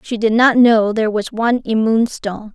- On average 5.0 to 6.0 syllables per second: Yes, 5.3 syllables/s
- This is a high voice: Yes, high, 225 Hz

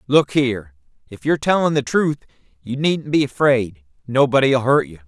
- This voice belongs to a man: Yes, male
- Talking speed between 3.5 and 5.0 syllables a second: No, 5.2 syllables/s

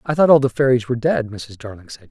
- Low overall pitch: Yes, low, 125 Hz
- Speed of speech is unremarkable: No, fast, 285 wpm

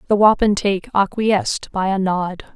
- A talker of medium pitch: No, high, 200 Hz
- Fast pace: No, average, 140 wpm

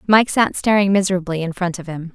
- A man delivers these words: No, female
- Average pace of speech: No, fast, 225 wpm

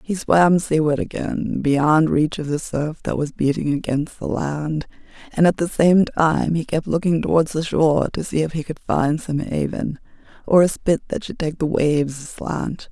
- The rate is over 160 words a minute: Yes, average, 200 wpm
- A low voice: No, medium, 160 Hz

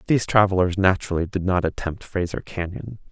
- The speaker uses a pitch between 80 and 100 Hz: Yes, very low, 95 Hz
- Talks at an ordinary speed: Yes, average, 155 wpm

